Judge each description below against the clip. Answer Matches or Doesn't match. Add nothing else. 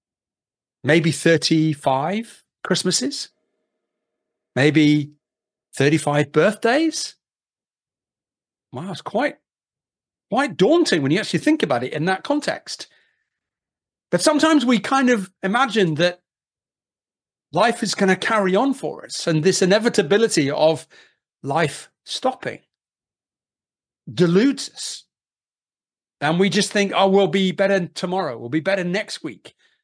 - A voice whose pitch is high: Matches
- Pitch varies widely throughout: Matches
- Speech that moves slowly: Matches